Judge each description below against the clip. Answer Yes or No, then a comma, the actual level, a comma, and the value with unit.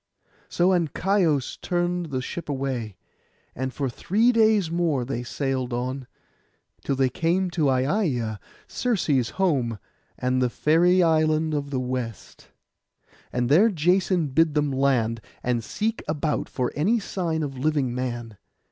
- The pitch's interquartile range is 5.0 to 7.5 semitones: Yes, wide, 5.4 semitones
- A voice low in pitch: No, medium, 145 Hz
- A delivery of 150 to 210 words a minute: No, average, 140 wpm